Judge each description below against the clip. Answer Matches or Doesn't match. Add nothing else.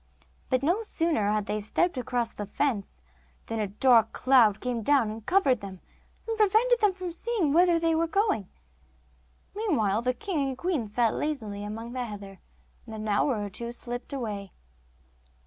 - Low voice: Doesn't match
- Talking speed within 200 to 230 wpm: Doesn't match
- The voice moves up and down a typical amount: Doesn't match